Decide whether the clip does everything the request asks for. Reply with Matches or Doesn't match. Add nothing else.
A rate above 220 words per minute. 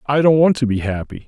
Matches